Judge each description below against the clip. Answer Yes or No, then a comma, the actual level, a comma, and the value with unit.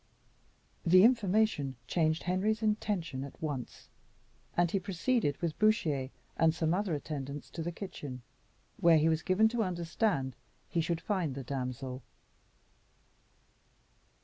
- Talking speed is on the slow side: Yes, slow, 125 wpm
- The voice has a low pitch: No, medium, 165 Hz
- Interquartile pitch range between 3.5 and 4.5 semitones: No, wide, 5.6 semitones